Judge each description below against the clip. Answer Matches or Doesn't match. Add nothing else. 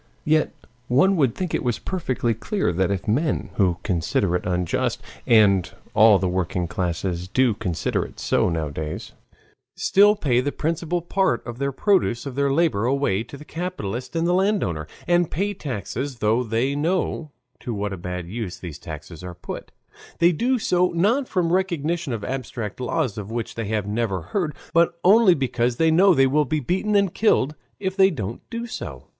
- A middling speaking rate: Matches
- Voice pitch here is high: Doesn't match